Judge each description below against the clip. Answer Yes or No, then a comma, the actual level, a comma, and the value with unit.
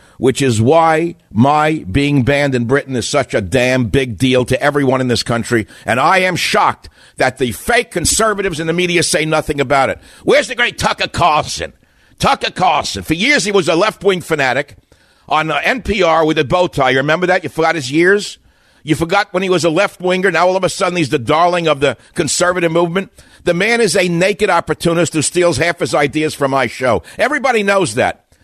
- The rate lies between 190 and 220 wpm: Yes, fast, 205 wpm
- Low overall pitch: No, medium, 160 Hz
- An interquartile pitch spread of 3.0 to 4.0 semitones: No, average, 4.7 semitones